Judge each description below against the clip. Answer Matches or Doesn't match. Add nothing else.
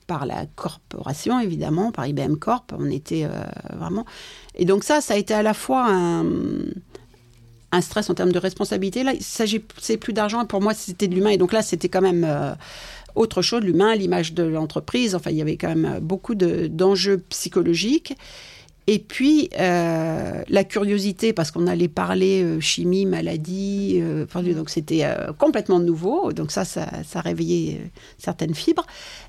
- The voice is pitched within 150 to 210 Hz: Matches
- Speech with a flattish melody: Doesn't match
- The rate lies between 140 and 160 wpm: Doesn't match